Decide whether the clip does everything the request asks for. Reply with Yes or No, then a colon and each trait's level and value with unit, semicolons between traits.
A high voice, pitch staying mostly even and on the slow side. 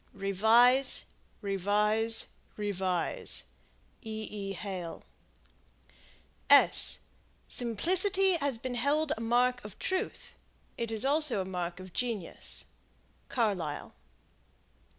No: high, 220 Hz; average, 4.3 semitones; slow, 90 wpm